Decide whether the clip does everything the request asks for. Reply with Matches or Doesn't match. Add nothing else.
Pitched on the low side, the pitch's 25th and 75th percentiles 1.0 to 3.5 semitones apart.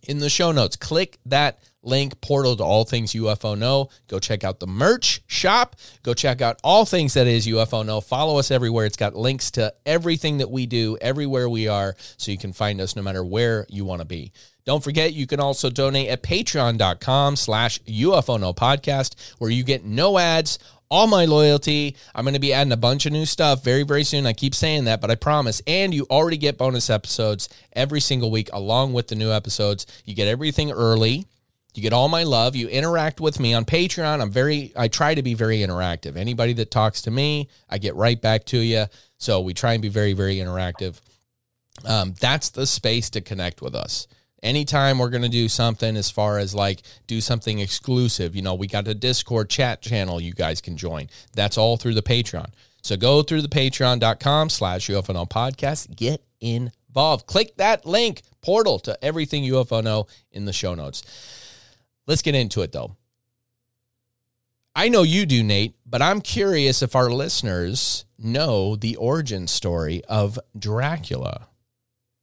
Doesn't match